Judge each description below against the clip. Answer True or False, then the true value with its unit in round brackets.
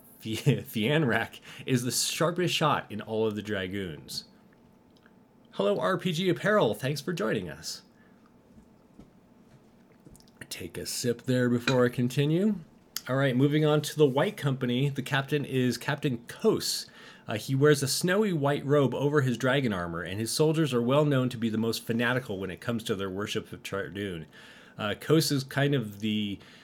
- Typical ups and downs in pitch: True (4.9 semitones)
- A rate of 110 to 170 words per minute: True (165 wpm)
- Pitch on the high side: False (130 Hz)